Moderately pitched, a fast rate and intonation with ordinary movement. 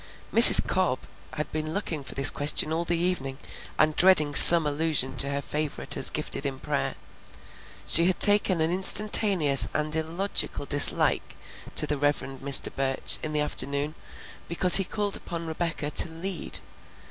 No: medium, 155 Hz; average, 160 wpm; average, 3.3 semitones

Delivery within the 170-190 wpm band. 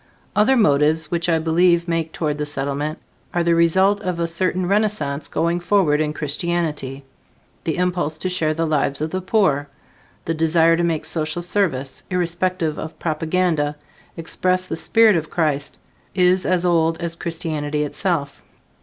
No: average, 155 wpm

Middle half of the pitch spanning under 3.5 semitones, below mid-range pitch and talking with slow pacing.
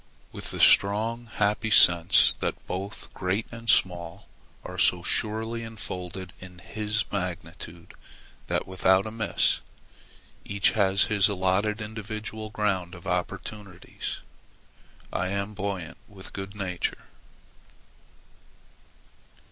Yes: average, 2.8 semitones; low, 100 Hz; slow, 110 wpm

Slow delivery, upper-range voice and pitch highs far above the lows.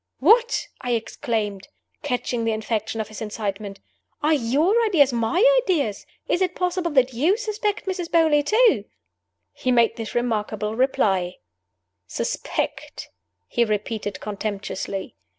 Yes: slow, 125 wpm; high, 240 Hz; wide, 8.0 semitones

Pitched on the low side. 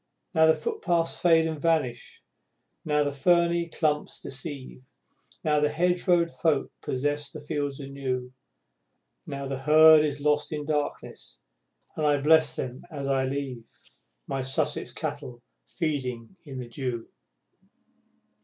No: medium, 145 Hz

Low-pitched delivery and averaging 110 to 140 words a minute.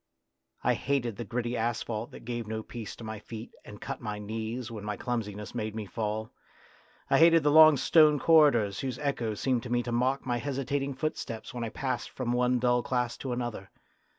No: low, 120 Hz; fast, 205 wpm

